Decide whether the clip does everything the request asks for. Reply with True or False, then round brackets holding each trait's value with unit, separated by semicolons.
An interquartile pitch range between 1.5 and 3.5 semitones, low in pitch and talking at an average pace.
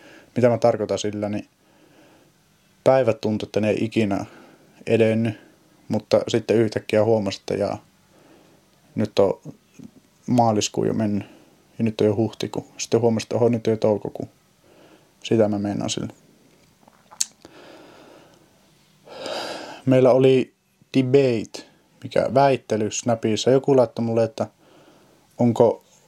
True (2.8 semitones; 115 Hz; 115 wpm)